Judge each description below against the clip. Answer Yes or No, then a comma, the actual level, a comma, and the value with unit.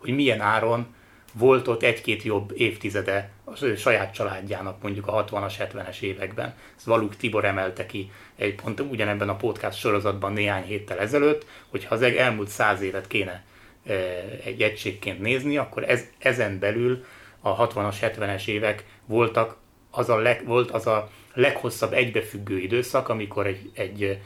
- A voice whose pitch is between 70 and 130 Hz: Yes, low, 105 Hz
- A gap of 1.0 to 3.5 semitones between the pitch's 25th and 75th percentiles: Yes, average, 2.8 semitones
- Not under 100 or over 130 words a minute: No, average, 150 wpm